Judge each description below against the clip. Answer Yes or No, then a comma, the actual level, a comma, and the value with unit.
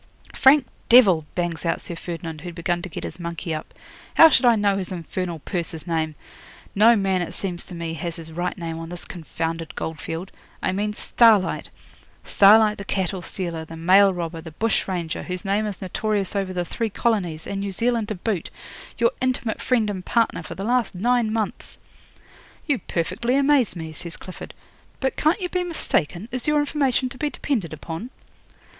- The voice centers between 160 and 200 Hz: Yes, high, 190 Hz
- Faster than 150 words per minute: Yes, average, 185 wpm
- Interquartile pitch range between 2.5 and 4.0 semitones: No, average, 5.1 semitones